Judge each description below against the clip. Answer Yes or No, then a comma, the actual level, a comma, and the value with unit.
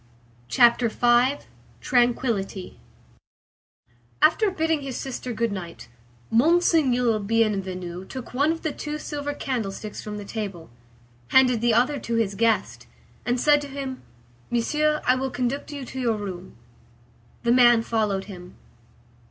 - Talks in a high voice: Yes, high, 240 Hz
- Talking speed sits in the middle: No, slow, 130 wpm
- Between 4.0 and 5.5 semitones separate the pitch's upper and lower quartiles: Yes, average, 4.4 semitones